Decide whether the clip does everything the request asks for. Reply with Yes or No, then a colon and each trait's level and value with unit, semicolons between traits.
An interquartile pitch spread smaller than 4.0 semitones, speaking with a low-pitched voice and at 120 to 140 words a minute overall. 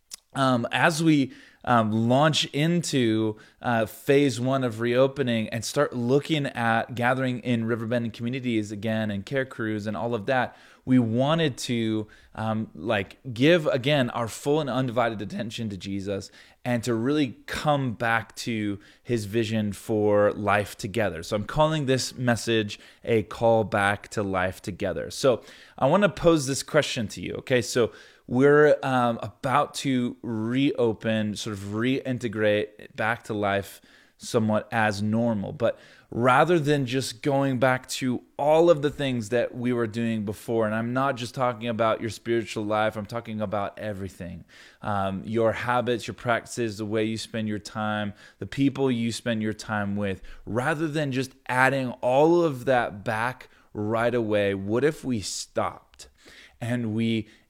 No: average, 3.4 semitones; low, 120 Hz; average, 160 wpm